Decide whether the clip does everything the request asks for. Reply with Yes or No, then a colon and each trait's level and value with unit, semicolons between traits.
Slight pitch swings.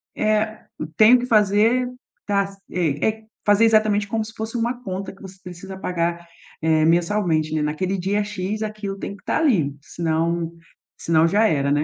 No: average, 4.2 semitones